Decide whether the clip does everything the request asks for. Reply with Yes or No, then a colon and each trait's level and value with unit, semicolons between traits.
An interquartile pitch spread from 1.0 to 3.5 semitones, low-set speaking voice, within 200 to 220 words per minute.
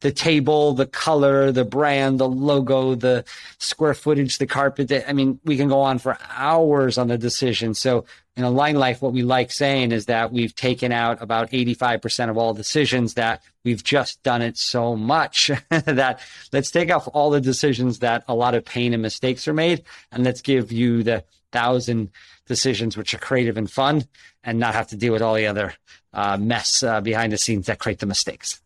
Yes: average, 3.0 semitones; low, 125 Hz; fast, 205 wpm